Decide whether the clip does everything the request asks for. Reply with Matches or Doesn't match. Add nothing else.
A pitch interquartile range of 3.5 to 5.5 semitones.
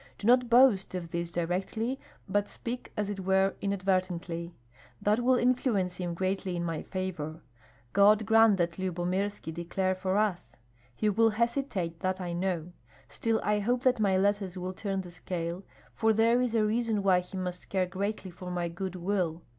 Doesn't match